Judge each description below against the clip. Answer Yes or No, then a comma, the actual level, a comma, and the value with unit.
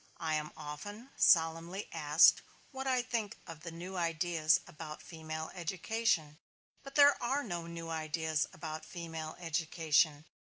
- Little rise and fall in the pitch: No, average, 3.1 semitones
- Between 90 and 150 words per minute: Yes, slow, 135 wpm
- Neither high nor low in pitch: Yes, medium, 165 Hz